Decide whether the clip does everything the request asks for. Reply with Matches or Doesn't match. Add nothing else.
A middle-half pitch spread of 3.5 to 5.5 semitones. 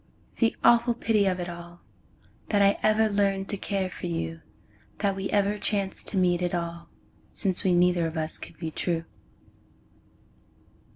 Doesn't match